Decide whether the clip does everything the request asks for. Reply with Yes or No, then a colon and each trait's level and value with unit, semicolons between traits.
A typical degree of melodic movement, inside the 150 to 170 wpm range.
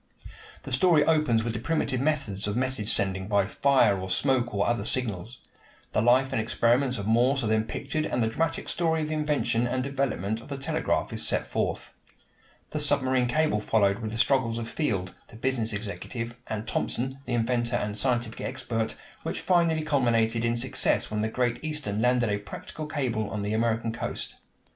No: average, 3.6 semitones; average, 185 wpm